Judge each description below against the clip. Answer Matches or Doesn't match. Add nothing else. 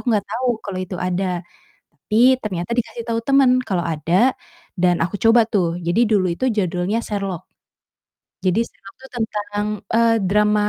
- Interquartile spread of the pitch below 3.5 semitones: Doesn't match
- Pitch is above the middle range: Matches